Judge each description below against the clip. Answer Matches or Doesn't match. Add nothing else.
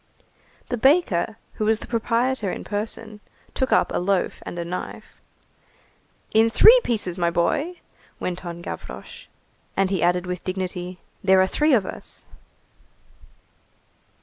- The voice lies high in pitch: Matches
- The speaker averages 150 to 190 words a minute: Doesn't match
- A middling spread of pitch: Matches